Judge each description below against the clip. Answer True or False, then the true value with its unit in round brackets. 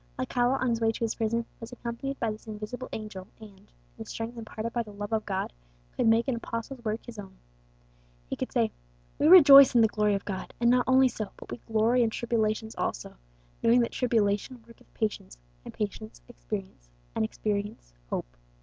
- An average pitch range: False (2.3 semitones)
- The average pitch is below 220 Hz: False (225 Hz)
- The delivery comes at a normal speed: True (195 wpm)